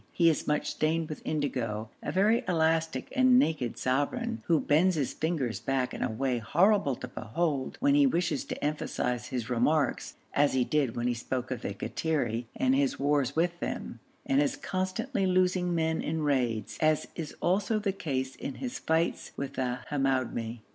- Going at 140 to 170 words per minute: No, average, 180 wpm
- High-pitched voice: No, medium, 145 Hz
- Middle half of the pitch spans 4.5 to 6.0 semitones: Yes, average, 5.1 semitones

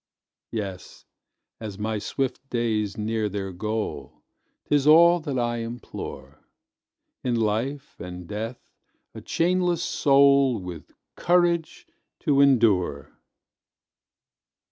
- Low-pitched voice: Yes, low, 115 Hz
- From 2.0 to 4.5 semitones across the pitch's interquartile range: No, average, 5.2 semitones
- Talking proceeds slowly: Yes, slow, 100 wpm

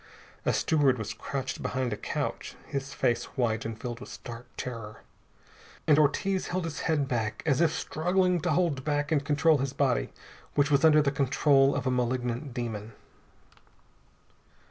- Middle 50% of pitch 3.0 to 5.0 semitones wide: Yes, average, 4.0 semitones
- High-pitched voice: No, medium, 140 Hz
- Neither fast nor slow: Yes, average, 165 wpm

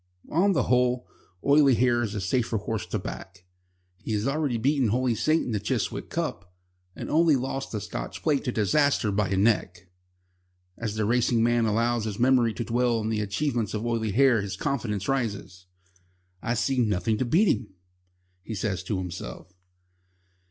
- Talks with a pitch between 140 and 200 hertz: No, low, 115 Hz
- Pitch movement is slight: No, average, 3.6 semitones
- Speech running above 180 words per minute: No, average, 175 wpm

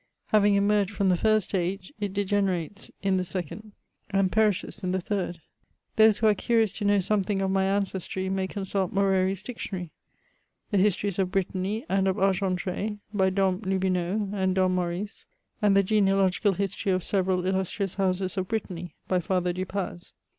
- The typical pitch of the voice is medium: No, high, 195 Hz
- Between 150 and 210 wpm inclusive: Yes, average, 170 wpm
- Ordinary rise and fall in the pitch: No, narrow, 1.7 semitones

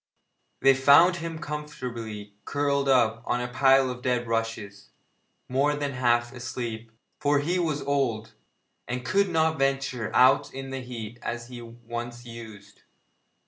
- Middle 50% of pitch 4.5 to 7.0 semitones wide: No, average, 3.2 semitones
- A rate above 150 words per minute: No, average, 145 wpm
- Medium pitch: No, low, 125 Hz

